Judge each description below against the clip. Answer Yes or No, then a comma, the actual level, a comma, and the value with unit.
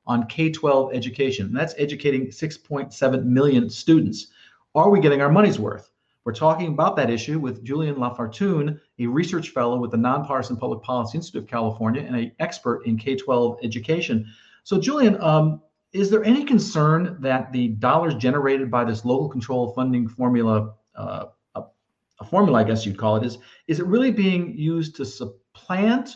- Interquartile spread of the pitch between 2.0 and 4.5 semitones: No, average, 5.0 semitones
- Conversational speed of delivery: Yes, average, 170 wpm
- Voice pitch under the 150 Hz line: Yes, low, 135 Hz